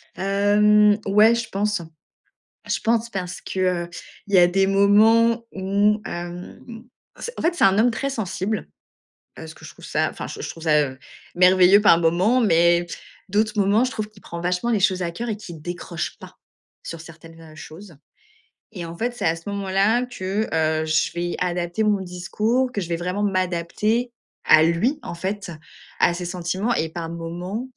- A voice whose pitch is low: No, high, 190 Hz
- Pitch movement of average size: Yes, average, 3.6 semitones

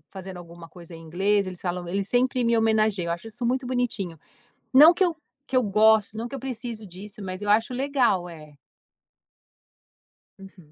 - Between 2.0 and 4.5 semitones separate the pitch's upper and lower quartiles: No, average, 5.2 semitones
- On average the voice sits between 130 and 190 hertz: No, high, 205 Hz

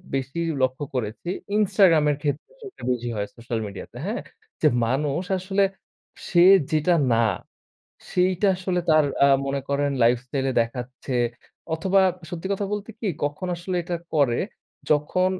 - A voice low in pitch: No, medium, 150 Hz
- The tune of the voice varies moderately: No, wide, 5.9 semitones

